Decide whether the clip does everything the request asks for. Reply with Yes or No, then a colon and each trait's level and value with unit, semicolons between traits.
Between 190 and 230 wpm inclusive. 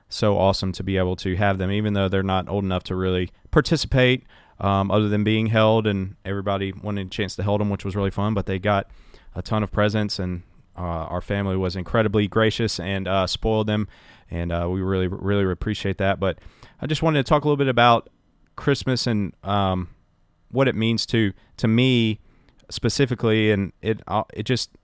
Yes: average, 200 wpm